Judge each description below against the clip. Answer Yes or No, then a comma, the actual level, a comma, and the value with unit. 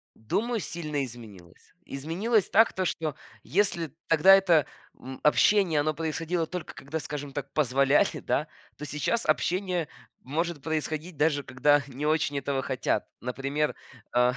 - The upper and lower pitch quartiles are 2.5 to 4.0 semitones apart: Yes, average, 3.6 semitones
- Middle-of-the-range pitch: Yes, medium, 150 Hz